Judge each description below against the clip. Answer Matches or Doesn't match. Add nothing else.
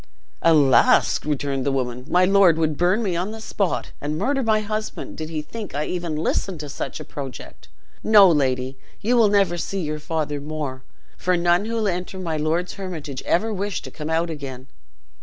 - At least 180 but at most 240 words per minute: Matches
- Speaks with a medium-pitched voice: Matches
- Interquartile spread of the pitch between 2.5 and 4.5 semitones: Doesn't match